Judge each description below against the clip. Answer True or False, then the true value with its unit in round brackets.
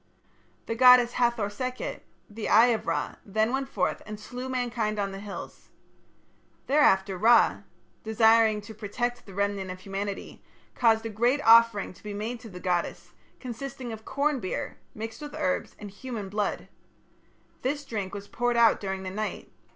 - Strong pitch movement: False (3.3 semitones)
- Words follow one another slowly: False (165 wpm)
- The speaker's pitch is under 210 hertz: False (220 Hz)